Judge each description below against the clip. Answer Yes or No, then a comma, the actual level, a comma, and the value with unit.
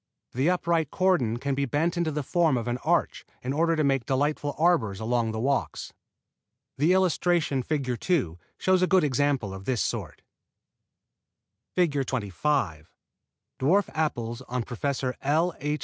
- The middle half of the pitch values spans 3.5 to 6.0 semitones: Yes, average, 5.2 semitones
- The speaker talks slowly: No, average, 155 wpm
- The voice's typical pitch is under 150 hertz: Yes, medium, 140 Hz